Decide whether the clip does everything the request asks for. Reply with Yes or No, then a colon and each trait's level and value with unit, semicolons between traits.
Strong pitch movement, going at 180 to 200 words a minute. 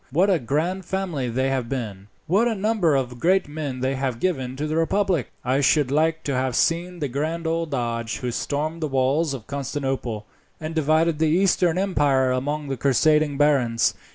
No: average, 4.0 semitones; average, 185 wpm